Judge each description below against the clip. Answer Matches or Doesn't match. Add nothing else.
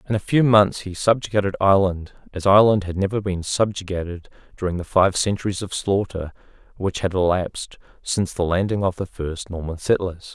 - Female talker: Doesn't match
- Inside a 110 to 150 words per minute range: Doesn't match